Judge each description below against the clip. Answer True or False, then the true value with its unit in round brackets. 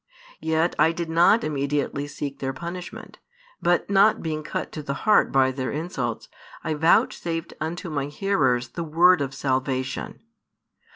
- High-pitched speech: False (155 Hz)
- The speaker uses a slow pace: False (150 wpm)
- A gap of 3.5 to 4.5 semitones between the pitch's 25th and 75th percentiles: True (3.8 semitones)